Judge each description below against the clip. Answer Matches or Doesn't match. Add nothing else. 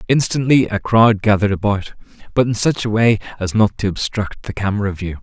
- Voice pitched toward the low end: Matches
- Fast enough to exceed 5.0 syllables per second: Matches